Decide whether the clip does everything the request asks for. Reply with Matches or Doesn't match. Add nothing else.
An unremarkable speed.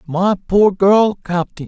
Matches